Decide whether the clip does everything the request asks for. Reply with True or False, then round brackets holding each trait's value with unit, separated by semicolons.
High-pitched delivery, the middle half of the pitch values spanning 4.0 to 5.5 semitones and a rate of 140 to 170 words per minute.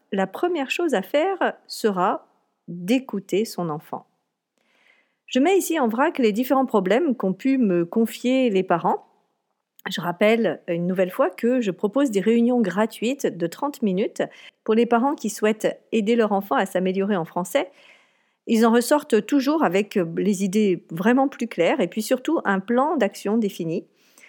True (225 Hz; 5.2 semitones; 165 wpm)